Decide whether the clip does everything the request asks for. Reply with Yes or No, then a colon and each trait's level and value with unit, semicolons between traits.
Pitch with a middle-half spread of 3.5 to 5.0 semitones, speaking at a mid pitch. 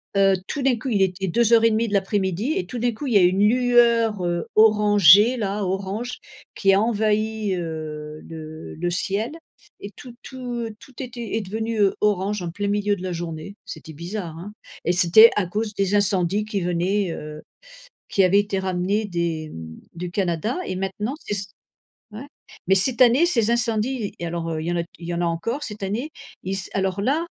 No: average, 4.0 semitones; high, 200 Hz